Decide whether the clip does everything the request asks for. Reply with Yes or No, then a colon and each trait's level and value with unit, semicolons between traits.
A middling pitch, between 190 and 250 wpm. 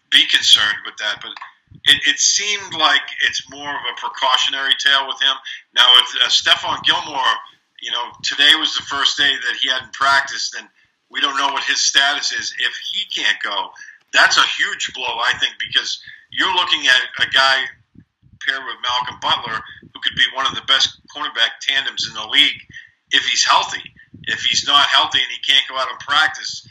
Yes: medium, 175 Hz; average, 195 wpm